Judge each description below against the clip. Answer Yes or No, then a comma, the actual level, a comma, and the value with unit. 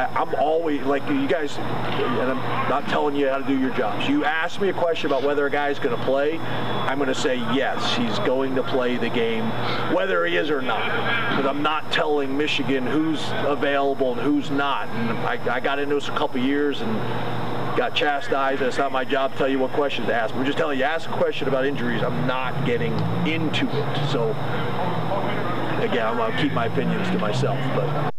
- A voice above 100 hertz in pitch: Yes, medium, 140 Hz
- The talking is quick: Yes, fast, 215 wpm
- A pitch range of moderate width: No, narrow, 2.0 semitones